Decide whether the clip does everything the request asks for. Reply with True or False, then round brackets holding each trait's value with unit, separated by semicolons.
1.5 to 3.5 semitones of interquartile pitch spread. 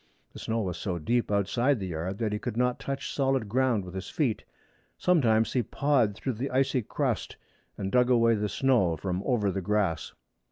False (4.5 semitones)